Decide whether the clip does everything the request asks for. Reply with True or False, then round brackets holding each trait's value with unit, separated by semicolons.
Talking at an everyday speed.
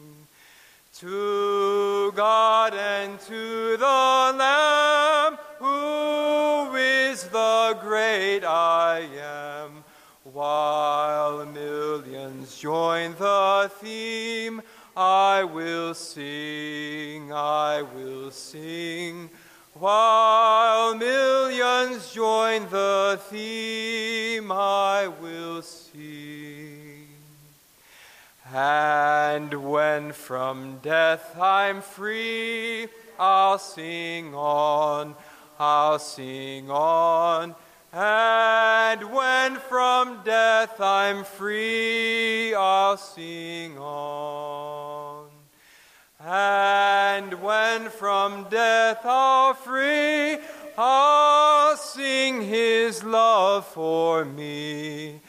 False (70 wpm)